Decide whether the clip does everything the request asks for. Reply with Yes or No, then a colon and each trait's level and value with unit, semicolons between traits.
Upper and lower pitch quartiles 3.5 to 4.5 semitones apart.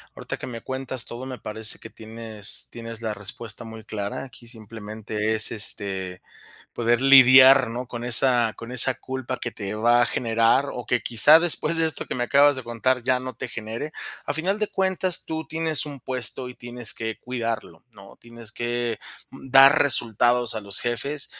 No: average, 2.8 semitones